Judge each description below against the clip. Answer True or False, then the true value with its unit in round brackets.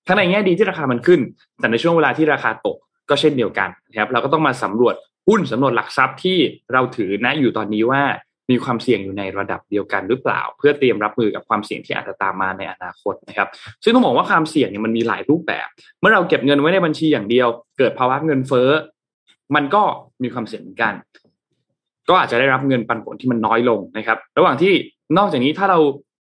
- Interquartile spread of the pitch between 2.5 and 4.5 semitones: False (5.0 semitones)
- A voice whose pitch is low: True (130 Hz)